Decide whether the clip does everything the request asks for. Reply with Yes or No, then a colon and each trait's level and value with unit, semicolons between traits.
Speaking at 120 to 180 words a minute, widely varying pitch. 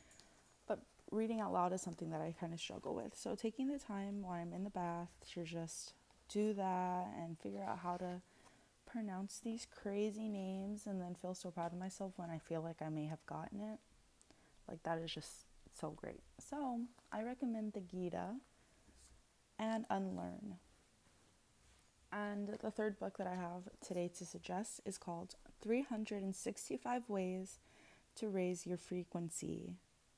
No: average, 160 wpm; average, 4.0 semitones